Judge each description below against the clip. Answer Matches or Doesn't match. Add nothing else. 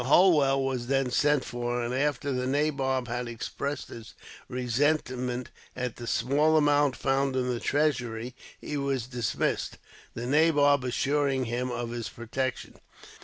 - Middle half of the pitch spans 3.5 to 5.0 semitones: Doesn't match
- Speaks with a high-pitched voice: Doesn't match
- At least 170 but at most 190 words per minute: Doesn't match